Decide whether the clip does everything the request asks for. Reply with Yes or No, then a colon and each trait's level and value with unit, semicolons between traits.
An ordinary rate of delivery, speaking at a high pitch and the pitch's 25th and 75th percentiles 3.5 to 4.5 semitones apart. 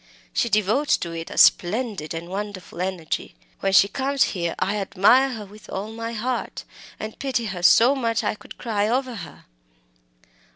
Yes: average, 175 wpm; high, 210 Hz; average, 3.9 semitones